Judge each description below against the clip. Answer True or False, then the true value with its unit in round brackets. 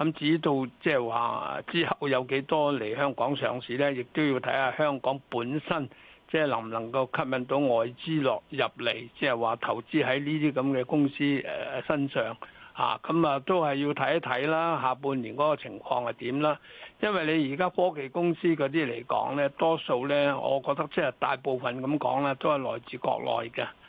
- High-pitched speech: False (140 Hz)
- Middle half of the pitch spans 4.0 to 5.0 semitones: False (2.9 semitones)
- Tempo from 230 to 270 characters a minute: False (280 characters per minute)